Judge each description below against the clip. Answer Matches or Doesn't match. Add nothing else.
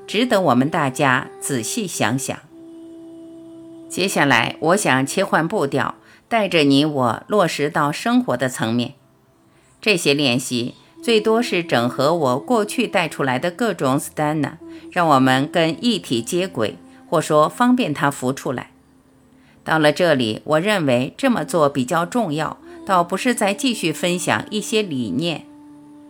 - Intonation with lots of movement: Matches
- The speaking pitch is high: Doesn't match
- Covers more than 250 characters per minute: Doesn't match